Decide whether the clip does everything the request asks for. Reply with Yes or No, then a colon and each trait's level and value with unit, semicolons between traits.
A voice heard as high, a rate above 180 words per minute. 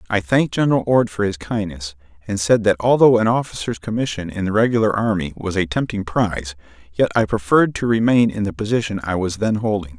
No: low, 105 Hz; fast, 205 wpm